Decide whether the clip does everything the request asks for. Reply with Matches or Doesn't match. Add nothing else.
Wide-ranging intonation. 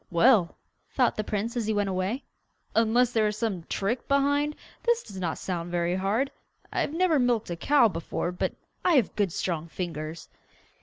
Matches